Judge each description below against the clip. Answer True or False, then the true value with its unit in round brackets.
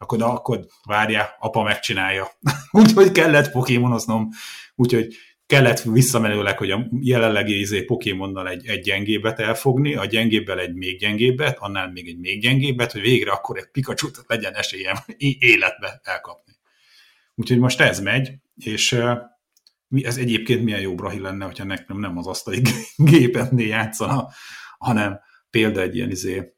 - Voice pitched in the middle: False (115 Hz)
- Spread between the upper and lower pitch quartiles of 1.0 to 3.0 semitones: False (3.5 semitones)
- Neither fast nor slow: True (140 wpm)